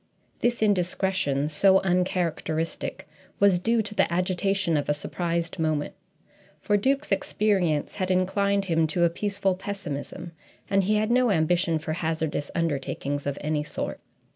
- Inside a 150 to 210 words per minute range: No, average, 140 wpm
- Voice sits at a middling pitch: Yes, medium, 180 Hz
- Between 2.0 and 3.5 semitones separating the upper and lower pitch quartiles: No, average, 4.0 semitones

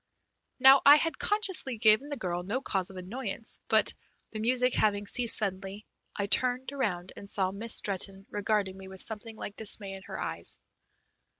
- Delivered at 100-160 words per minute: No, average, 175 wpm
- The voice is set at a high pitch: Yes, high, 215 Hz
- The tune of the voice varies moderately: Yes, average, 4.5 semitones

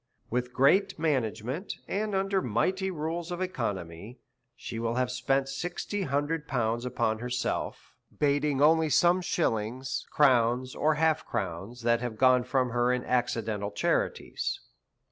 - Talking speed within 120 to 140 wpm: Yes, slow, 135 wpm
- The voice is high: No, low, 130 Hz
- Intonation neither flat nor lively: Yes, average, 5.0 semitones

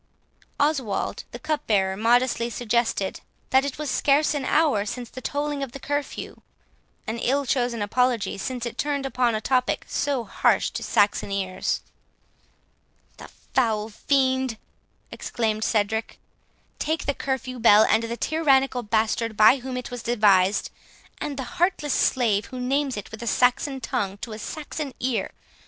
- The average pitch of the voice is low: No, high, 245 Hz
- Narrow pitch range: No, average, 3.8 semitones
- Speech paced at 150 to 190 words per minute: Yes, average, 155 wpm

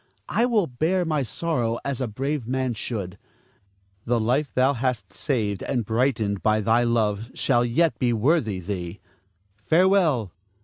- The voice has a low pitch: Yes, low, 120 Hz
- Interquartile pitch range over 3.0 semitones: Yes, average, 4.6 semitones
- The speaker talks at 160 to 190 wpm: No, average, 145 wpm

